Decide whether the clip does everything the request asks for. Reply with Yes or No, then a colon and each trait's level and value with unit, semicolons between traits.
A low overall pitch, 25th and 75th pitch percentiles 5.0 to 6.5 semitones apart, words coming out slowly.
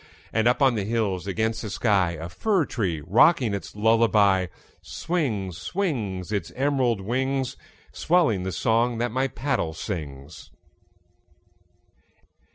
Yes: low, 110 Hz; wide, 5.6 semitones; slow, 125 wpm